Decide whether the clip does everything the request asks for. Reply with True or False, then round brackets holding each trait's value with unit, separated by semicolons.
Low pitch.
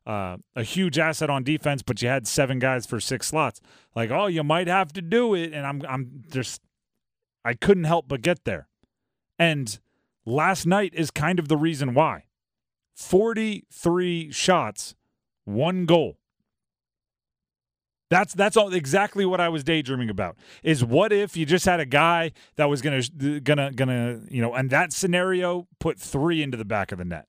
False (155 Hz)